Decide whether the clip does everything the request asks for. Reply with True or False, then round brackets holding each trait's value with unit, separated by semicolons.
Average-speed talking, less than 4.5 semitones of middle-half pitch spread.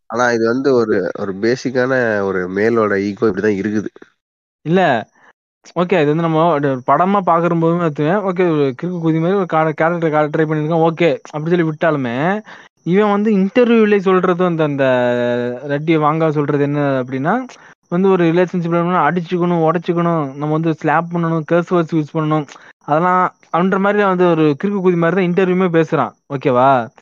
False (150 wpm; 3.9 semitones)